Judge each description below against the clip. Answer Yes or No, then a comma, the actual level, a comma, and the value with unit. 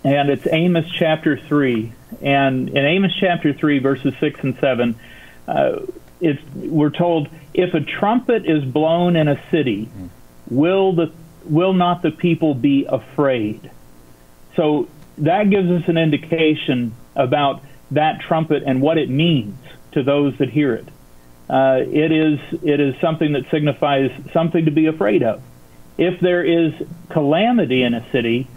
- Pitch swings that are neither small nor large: Yes, average, 3.8 semitones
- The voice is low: No, medium, 150 Hz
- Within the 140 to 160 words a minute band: Yes, average, 150 wpm